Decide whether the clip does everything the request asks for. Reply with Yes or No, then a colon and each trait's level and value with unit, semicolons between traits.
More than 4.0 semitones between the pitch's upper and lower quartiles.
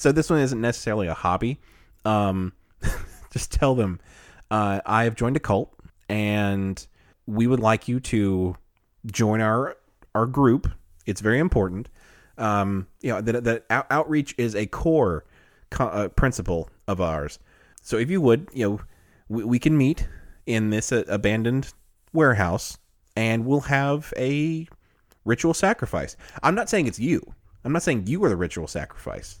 Yes: average, 4.7 semitones